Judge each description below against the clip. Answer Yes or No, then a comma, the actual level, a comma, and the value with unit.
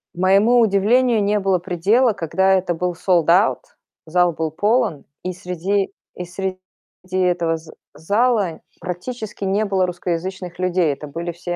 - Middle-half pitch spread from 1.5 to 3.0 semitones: Yes, average, 2.7 semitones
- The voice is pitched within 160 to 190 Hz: Yes, medium, 185 Hz